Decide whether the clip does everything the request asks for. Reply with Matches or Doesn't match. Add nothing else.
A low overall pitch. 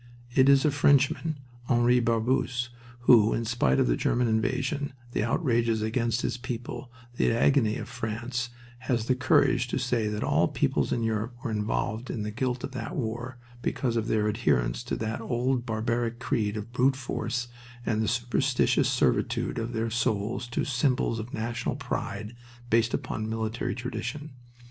Matches